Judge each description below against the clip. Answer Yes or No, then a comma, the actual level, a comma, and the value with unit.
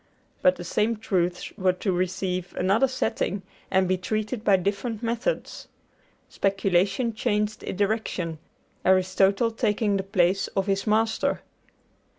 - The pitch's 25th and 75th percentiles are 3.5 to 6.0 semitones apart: No, average, 2.7 semitones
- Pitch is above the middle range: Yes, high, 195 Hz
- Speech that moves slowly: Yes, slow, 130 wpm